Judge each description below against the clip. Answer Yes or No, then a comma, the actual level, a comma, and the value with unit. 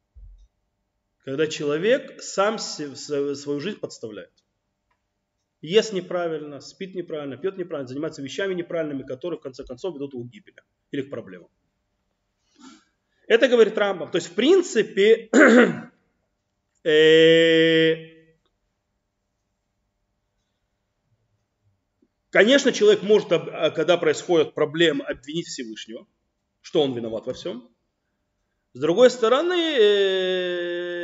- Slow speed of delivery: Yes, slow, 95 wpm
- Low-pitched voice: No, medium, 150 Hz